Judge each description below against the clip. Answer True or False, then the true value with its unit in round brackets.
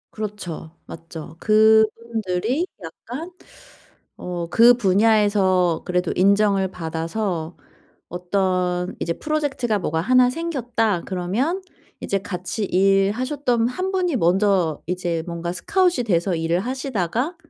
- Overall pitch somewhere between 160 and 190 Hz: False (200 Hz)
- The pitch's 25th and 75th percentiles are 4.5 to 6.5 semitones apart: True (5.2 semitones)